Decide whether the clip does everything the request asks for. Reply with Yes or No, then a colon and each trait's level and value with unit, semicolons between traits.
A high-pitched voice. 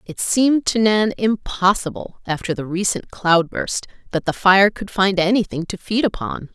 Yes: high, 195 Hz